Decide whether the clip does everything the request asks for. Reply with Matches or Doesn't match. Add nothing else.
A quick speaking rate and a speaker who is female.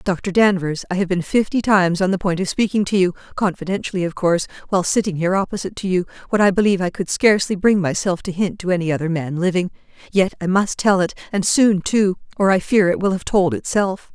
Matches